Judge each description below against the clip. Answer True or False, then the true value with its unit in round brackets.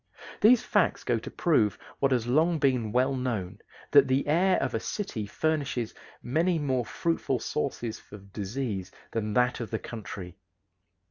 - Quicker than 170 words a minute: False (155 wpm)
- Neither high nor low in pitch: False (125 Hz)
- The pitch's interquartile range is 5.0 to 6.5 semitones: True (5.5 semitones)